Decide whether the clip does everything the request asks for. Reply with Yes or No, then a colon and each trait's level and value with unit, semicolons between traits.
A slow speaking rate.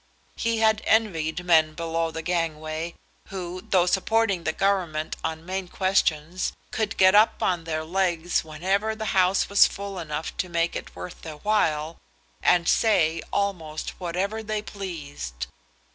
No: average, 145 wpm